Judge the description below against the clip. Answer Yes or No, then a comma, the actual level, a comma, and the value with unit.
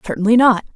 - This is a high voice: Yes, high, 225 Hz